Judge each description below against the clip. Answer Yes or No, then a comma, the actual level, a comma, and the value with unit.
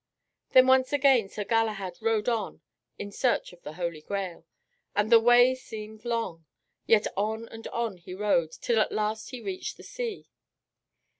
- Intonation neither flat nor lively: Yes, average, 3.5 semitones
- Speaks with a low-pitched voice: No, high, 220 Hz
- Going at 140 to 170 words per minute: Yes, average, 165 wpm